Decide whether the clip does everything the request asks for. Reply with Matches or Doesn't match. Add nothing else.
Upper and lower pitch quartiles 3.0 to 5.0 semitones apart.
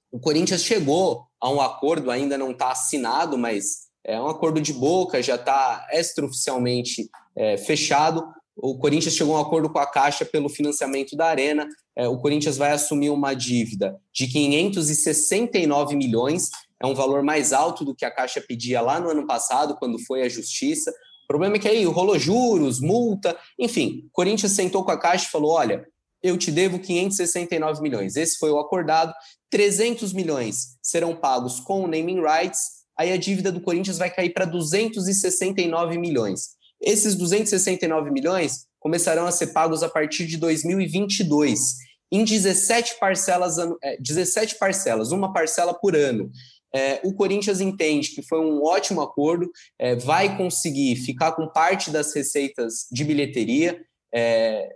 Matches